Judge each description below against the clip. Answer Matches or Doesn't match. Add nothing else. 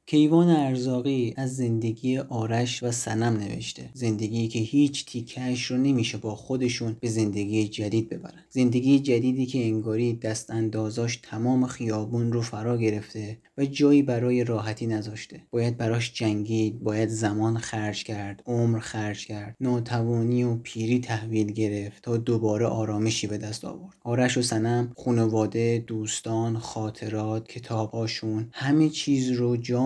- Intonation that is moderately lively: Doesn't match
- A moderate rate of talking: Matches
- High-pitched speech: Doesn't match